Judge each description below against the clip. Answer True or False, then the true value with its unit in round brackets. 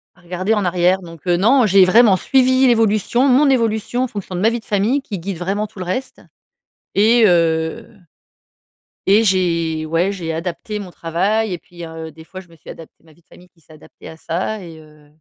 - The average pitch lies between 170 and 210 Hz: True (185 Hz)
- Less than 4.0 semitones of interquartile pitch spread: False (4.6 semitones)